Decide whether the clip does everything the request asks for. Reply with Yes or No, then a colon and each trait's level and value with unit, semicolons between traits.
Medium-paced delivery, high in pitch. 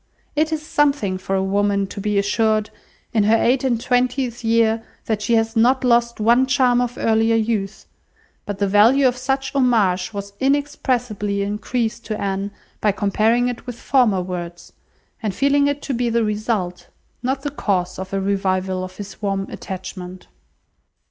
Yes: average, 170 wpm; high, 220 Hz